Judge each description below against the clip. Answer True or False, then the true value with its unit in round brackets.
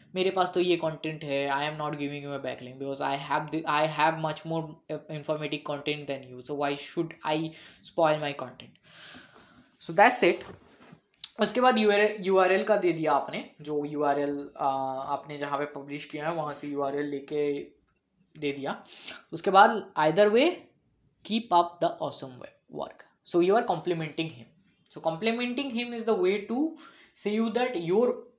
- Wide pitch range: True (5.8 semitones)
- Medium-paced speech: False (115 wpm)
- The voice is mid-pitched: True (155 Hz)